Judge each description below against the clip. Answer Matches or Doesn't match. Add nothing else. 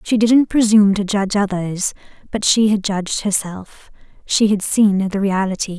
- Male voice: Doesn't match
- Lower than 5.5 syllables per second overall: Matches